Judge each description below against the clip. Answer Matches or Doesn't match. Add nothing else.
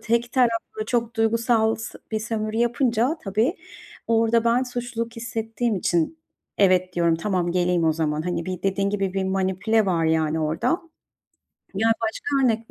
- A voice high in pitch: Matches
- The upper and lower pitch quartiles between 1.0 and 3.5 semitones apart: Doesn't match